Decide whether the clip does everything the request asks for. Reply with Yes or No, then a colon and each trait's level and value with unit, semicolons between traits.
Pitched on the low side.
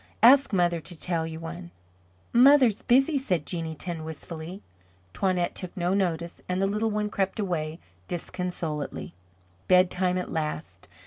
No: medium, 180 Hz